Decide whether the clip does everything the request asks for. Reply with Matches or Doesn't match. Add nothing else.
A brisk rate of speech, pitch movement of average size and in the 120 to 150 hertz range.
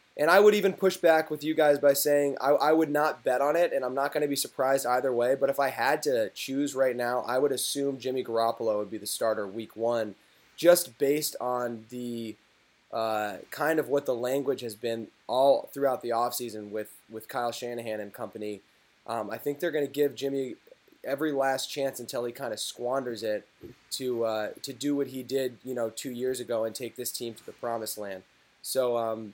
Matches